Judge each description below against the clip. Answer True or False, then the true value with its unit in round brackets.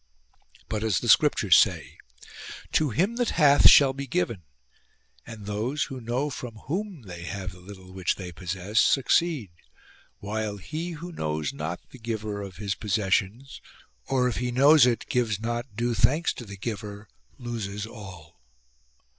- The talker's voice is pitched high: False (110 Hz)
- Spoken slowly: False (160 wpm)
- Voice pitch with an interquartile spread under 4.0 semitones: False (5.1 semitones)